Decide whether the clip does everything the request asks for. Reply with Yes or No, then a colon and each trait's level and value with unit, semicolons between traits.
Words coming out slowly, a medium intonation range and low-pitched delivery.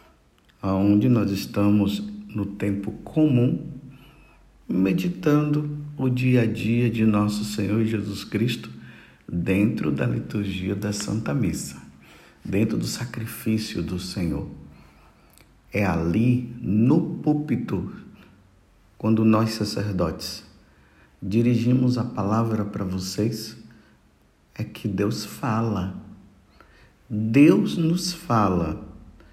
Yes: slow, 95 wpm; average, 3.3 semitones; low, 110 Hz